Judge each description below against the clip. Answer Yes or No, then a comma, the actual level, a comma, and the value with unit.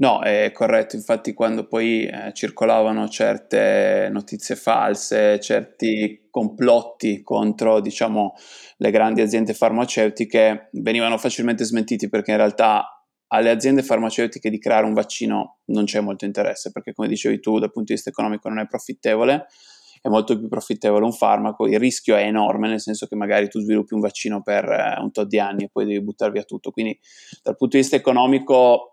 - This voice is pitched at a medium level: No, low, 110 Hz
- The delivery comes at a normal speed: No, fast, 175 wpm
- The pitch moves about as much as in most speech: No, narrow, 1.8 semitones